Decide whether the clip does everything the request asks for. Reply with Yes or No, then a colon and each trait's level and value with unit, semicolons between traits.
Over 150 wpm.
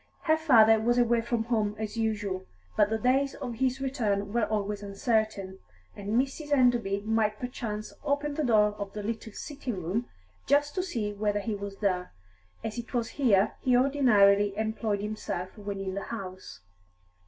Yes: average, 170 wpm